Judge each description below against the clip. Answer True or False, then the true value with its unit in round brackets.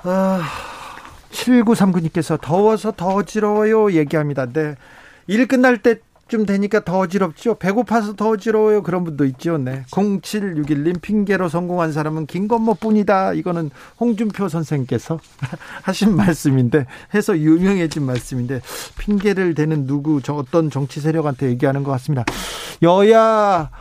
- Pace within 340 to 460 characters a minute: False (300 characters per minute)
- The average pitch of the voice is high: False (180 Hz)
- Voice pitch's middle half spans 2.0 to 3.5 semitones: False (5.6 semitones)